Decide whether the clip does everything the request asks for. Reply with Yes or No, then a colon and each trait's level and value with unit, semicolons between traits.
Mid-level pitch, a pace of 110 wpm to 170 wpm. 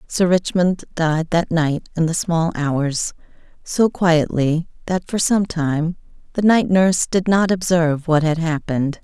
Yes: medium, 170 Hz; average, 160 wpm